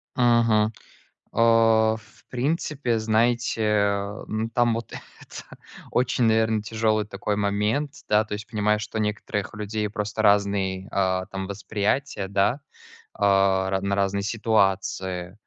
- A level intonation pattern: Yes, narrow, 2.2 semitones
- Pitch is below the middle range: Yes, low, 105 Hz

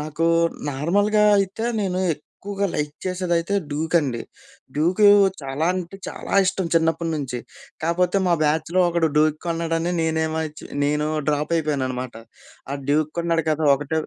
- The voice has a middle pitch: Yes, medium, 160 Hz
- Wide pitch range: No, average, 2.8 semitones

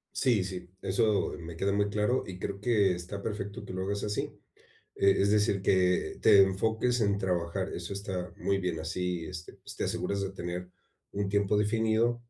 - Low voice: Yes, low, 100 Hz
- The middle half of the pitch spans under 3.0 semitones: Yes, narrow, 2.4 semitones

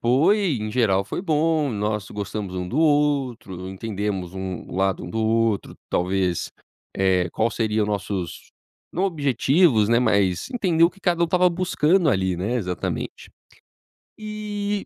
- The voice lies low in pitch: Yes, low, 115 Hz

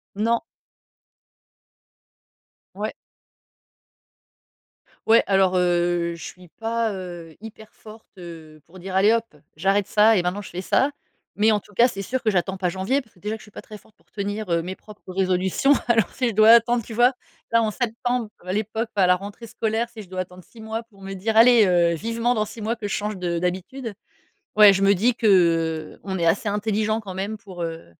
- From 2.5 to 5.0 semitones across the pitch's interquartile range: Yes, average, 3.6 semitones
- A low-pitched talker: No, high, 205 Hz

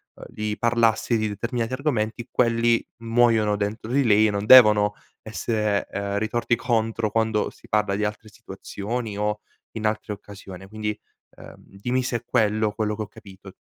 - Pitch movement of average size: No, narrow, 1.9 semitones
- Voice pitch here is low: Yes, low, 110 Hz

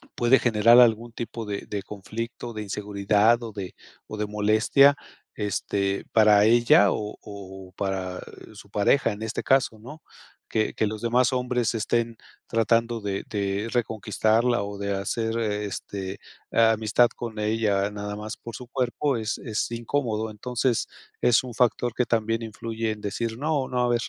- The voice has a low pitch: Yes, low, 110 Hz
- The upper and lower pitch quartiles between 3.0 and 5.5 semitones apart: No, narrow, 2.4 semitones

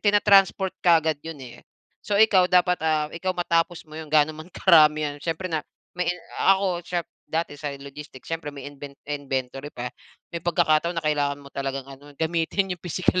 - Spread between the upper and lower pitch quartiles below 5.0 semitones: Yes, average, 3.3 semitones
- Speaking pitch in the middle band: Yes, medium, 160 Hz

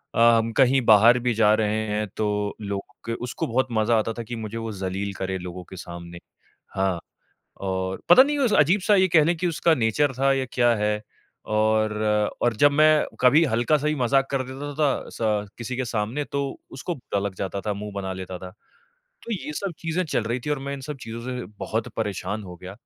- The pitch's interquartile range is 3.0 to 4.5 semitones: No, average, 5.1 semitones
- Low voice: Yes, low, 115 Hz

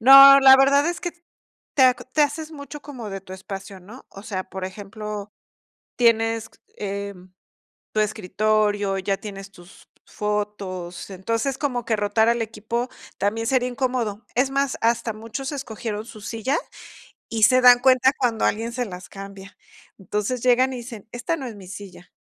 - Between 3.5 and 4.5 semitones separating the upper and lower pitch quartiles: Yes, average, 4.0 semitones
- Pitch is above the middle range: Yes, high, 225 Hz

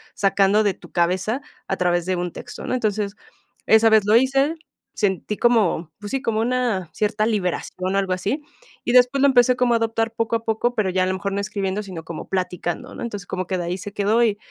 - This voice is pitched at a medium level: No, high, 205 Hz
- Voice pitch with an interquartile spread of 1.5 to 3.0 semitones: No, average, 3.6 semitones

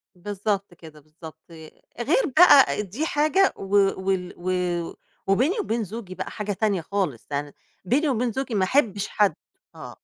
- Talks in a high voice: Yes, high, 200 Hz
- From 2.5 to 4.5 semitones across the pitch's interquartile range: No, wide, 5.4 semitones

